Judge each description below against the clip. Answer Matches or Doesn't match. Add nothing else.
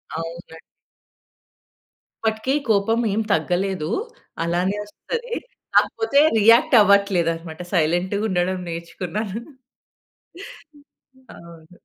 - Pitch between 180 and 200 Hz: Matches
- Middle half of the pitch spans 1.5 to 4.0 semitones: Doesn't match